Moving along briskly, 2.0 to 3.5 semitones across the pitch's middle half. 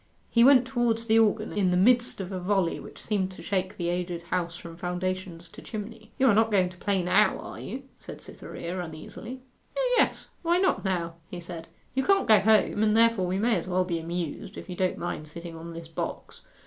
No: fast, 220 wpm; average, 4.3 semitones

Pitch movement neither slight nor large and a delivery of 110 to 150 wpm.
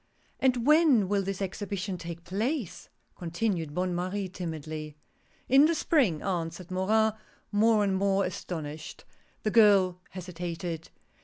Yes: average, 3.7 semitones; average, 140 wpm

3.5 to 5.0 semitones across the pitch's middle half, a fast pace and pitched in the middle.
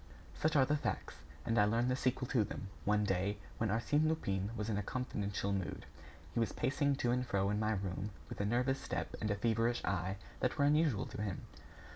No: average, 4.1 semitones; fast, 215 wpm; low, 110 Hz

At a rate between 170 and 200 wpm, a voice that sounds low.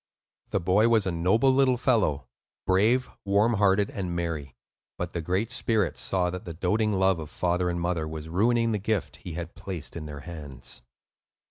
Yes: average, 185 wpm; very low, 90 Hz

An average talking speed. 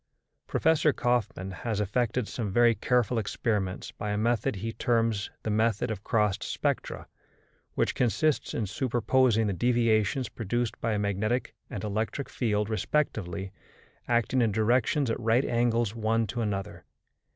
Yes: average, 145 wpm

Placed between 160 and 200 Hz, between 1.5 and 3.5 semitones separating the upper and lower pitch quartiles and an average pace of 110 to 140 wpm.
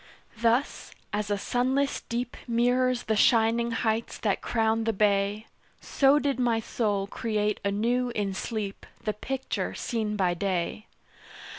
No: high, 225 Hz; average, 2.9 semitones; slow, 135 wpm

